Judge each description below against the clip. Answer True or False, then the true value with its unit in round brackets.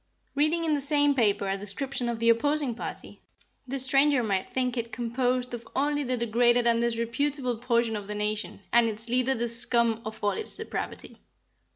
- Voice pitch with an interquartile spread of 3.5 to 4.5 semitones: False (2.8 semitones)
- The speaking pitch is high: True (240 Hz)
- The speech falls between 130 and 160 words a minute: False (185 wpm)